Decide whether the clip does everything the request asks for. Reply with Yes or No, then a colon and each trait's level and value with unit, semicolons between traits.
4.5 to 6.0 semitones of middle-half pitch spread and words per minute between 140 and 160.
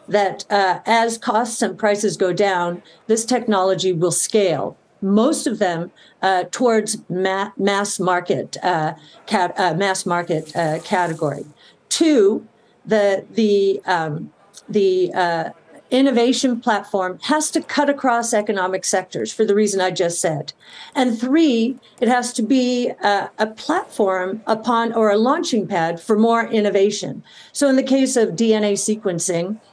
No: average, 4.1 semitones; average, 145 wpm